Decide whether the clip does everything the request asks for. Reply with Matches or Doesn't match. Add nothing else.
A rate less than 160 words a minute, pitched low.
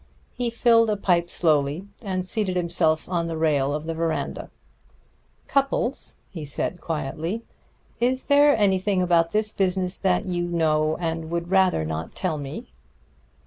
Doesn't match